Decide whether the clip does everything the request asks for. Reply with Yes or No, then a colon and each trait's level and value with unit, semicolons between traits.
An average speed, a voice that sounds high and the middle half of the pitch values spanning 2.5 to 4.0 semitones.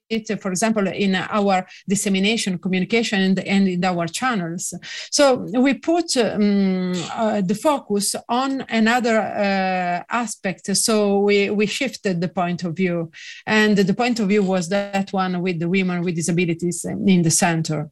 Yes: average, 155 wpm; high, 200 Hz; average, 3.2 semitones